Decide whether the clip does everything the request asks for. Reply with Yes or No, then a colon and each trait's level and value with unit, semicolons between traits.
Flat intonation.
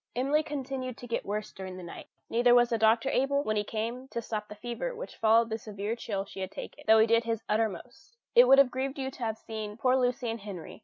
No: average, 3.3 semitones